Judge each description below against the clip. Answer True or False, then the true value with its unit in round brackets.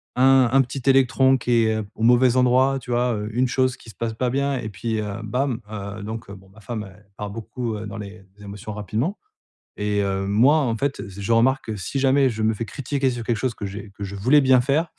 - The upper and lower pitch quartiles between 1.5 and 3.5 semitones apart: False (3.9 semitones)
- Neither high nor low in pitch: False (115 Hz)